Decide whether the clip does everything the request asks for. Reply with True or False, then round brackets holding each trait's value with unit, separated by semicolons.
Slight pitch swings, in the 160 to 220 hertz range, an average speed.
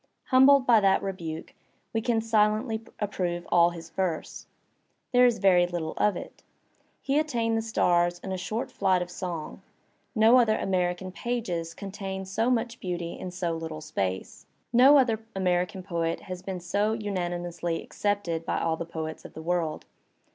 False (4.2 semitones; 185 Hz; 170 wpm)